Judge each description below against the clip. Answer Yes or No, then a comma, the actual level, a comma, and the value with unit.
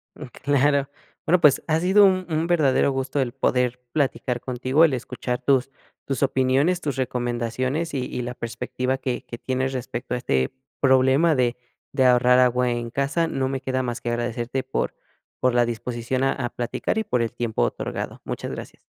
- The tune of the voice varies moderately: No, narrow, 2.2 semitones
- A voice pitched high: No, low, 130 Hz